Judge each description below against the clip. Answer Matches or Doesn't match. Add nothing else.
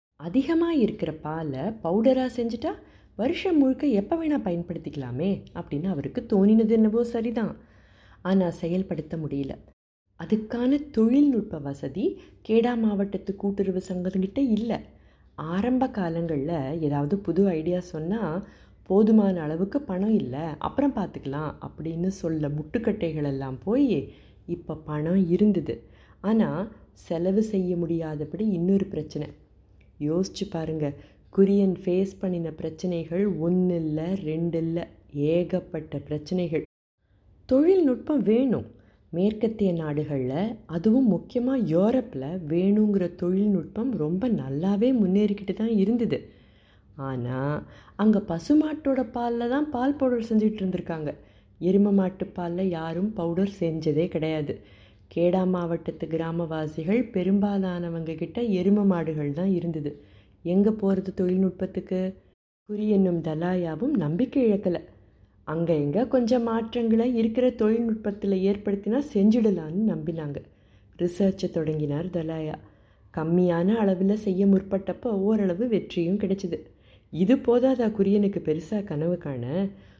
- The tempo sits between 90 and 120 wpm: Matches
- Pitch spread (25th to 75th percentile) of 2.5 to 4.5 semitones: Doesn't match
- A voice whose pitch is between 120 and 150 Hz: Doesn't match